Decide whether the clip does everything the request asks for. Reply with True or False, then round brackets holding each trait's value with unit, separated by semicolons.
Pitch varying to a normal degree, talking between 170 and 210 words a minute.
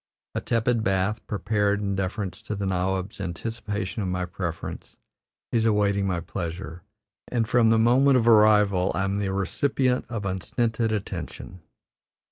False (3.1 semitones; 145 wpm)